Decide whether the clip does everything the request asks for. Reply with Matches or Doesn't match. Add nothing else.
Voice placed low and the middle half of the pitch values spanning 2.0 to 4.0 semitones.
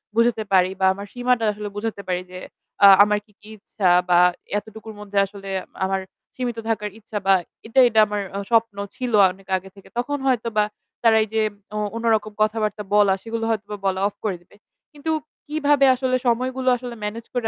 Doesn't match